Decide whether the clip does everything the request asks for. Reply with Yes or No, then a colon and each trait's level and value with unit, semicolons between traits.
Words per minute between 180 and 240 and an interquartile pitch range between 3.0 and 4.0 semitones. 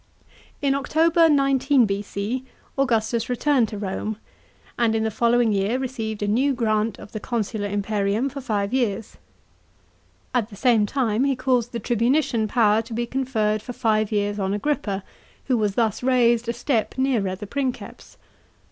No: average, 160 wpm; average, 3.6 semitones